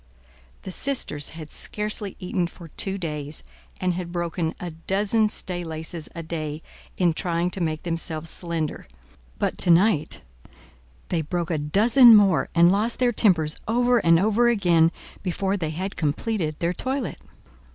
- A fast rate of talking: No, average, 150 wpm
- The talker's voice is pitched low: No, medium, 175 Hz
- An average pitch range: Yes, average, 3.9 semitones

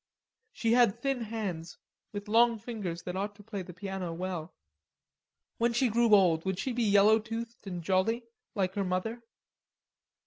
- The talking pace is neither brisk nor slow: Yes, average, 165 wpm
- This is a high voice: Yes, high, 205 Hz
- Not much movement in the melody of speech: No, average, 3.7 semitones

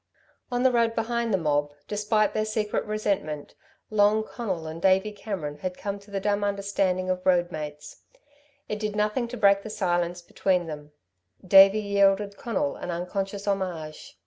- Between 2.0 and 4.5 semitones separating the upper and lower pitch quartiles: Yes, average, 3.1 semitones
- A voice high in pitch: Yes, high, 200 Hz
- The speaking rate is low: No, average, 165 wpm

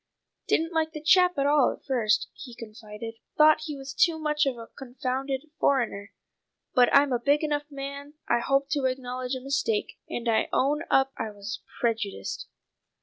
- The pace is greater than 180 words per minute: No, average, 175 wpm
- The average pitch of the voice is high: Yes, very high, 270 Hz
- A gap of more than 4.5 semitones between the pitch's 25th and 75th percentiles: No, average, 3.7 semitones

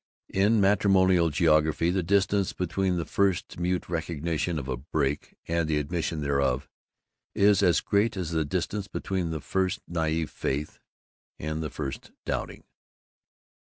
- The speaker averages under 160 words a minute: Yes, average, 140 wpm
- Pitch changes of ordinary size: Yes, average, 3.7 semitones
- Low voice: Yes, very low, 85 Hz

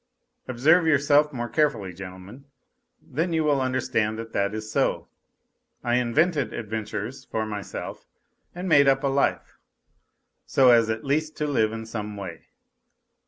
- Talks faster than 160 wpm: No, average, 145 wpm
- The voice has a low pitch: Yes, low, 125 Hz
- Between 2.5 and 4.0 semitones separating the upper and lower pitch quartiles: No, average, 4.9 semitones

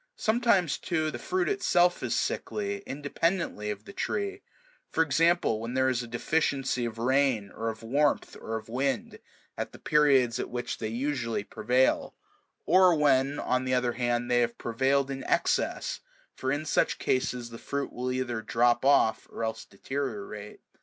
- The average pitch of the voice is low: Yes, low, 130 Hz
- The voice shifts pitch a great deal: No, average, 4.6 semitones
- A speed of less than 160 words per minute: No, average, 165 wpm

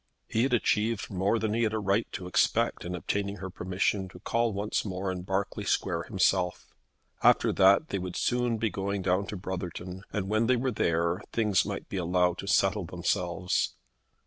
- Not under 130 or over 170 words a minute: No, average, 190 wpm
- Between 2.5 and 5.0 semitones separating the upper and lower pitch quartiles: Yes, average, 2.8 semitones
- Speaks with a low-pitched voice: Yes, very low, 95 Hz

